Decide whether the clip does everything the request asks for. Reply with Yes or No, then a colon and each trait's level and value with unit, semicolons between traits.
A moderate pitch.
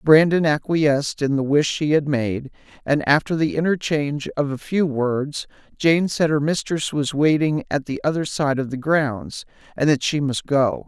Yes: medium, 145 Hz